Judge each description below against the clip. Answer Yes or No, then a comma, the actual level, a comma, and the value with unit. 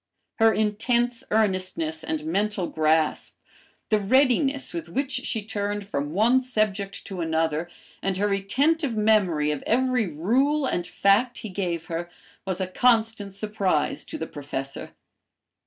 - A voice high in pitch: Yes, high, 200 Hz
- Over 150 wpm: No, average, 140 wpm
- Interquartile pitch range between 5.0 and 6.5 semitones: Yes, wide, 5.4 semitones